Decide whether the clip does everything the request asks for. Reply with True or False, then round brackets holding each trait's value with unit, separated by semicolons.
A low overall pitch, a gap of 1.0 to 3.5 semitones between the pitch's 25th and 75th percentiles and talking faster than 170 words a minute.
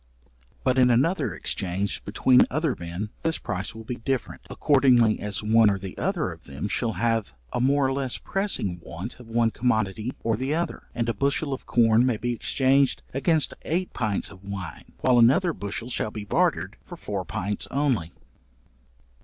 False (115 Hz; 4.7 semitones; 180 wpm)